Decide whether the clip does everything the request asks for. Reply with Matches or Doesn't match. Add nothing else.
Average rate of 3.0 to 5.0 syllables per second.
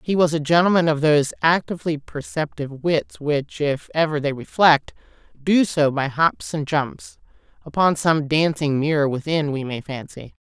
Matches